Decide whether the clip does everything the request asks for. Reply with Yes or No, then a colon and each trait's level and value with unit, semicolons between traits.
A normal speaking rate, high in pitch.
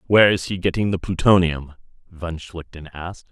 No: average, 145 wpm; very low, 85 Hz